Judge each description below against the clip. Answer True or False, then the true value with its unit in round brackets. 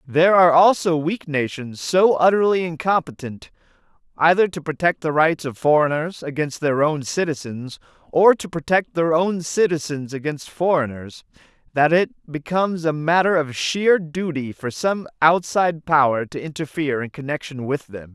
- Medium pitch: True (155 Hz)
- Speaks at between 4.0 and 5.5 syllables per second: True (4.8 syllables/s)